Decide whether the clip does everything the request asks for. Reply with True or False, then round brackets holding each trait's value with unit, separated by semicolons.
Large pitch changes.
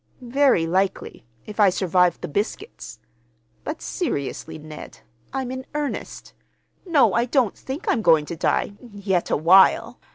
True (7.7 semitones)